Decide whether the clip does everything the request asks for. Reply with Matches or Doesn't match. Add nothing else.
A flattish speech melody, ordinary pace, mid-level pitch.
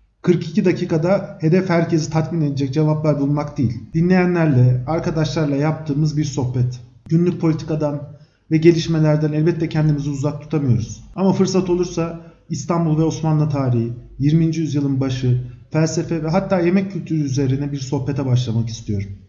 Doesn't match